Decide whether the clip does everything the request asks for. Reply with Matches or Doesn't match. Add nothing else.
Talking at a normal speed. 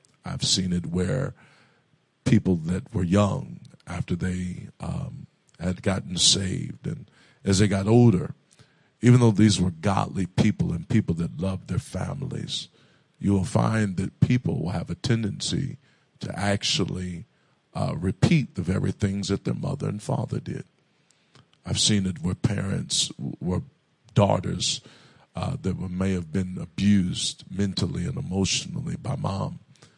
Matches